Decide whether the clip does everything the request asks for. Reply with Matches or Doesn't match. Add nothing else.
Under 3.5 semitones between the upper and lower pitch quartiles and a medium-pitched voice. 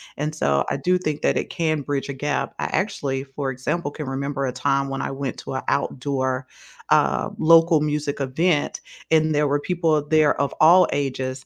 Matches